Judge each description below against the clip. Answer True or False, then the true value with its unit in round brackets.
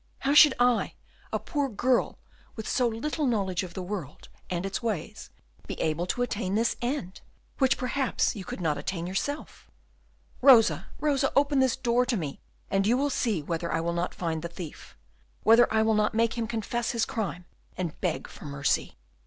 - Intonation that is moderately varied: False (5.9 semitones)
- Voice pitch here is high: True (220 Hz)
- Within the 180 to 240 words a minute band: True (185 wpm)